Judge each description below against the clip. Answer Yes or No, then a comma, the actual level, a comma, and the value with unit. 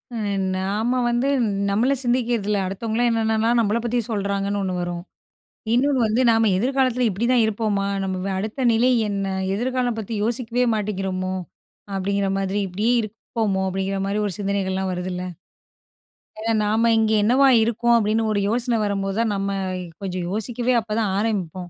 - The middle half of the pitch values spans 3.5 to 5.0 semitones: No, average, 3.1 semitones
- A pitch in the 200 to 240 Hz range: Yes, high, 215 Hz